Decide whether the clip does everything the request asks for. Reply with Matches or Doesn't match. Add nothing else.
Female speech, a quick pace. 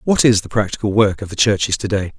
Doesn't match